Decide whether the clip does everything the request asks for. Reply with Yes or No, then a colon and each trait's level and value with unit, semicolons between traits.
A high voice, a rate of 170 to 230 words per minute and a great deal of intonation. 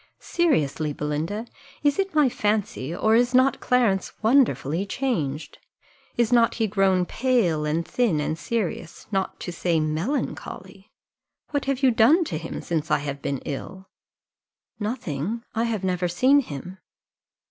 No: high, 195 Hz; average, 145 wpm; wide, 7.5 semitones